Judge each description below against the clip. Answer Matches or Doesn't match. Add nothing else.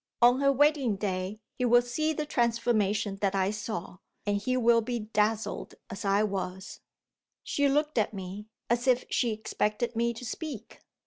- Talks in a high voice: Matches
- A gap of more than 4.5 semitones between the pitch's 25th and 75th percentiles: Doesn't match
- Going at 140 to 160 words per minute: Doesn't match